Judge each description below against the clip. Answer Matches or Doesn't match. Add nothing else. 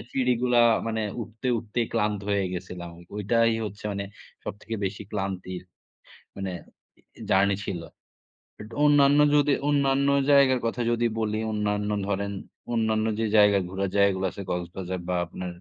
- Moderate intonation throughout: Matches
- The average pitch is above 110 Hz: Doesn't match